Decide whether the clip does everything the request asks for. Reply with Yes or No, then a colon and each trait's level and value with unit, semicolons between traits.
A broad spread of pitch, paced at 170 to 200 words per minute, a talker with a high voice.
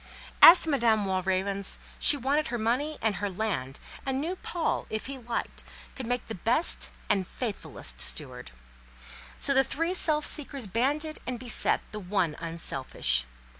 No: wide, 6.5 semitones; average, 155 wpm; high, 235 Hz